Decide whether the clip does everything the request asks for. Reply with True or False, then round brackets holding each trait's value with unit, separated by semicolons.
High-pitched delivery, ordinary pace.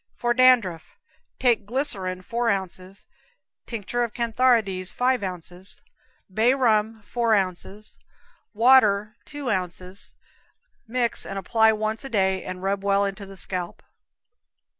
False (210 Hz; 120 wpm)